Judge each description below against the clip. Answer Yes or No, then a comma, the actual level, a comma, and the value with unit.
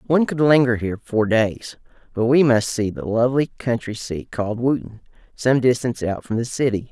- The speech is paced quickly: No, average, 190 wpm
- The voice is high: No, low, 120 Hz